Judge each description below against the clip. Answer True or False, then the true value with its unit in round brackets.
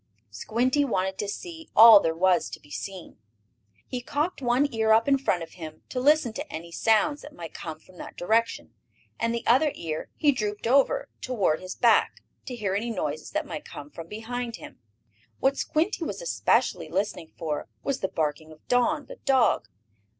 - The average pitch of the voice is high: True (225 Hz)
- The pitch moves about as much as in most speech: False (7.6 semitones)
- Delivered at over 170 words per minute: True (185 wpm)